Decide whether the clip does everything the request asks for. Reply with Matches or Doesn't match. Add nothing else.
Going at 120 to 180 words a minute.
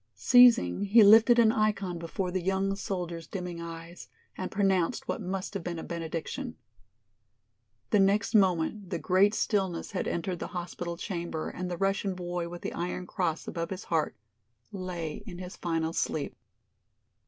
Matches